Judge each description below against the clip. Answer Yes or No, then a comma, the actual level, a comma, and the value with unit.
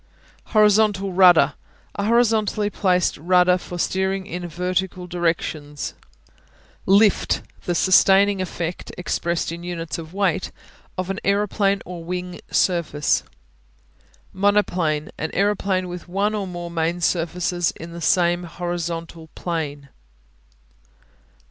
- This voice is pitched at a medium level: Yes, medium, 180 Hz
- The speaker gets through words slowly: Yes, slow, 110 wpm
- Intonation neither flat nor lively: No, narrow, 2.3 semitones